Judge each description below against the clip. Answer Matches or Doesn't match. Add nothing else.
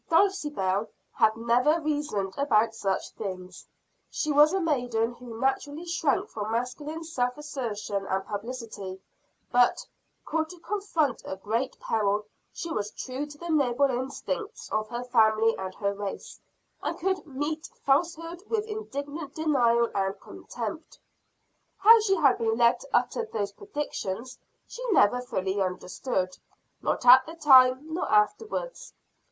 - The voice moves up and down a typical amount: Doesn't match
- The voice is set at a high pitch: Matches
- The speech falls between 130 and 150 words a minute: Matches